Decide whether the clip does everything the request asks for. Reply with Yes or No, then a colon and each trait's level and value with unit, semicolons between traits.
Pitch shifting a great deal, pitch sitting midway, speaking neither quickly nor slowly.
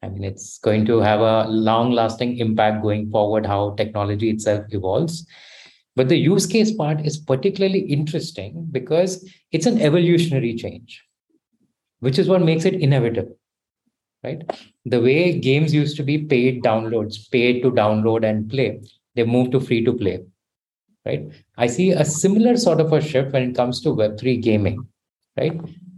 No: wide, 6.6 semitones; low, 125 Hz; average, 165 wpm